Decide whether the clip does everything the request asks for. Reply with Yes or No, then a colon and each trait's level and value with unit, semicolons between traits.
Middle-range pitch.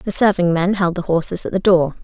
Yes: medium, 180 Hz